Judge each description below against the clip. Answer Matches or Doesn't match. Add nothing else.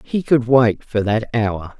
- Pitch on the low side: Matches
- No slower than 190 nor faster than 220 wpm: Matches